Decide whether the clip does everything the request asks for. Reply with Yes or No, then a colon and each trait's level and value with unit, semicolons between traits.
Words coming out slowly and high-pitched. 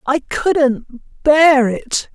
Yes: slow, 110 wpm; very high, 270 Hz